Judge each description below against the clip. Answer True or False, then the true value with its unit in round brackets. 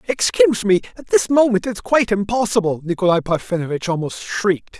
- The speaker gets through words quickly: False (150 wpm)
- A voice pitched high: True (195 Hz)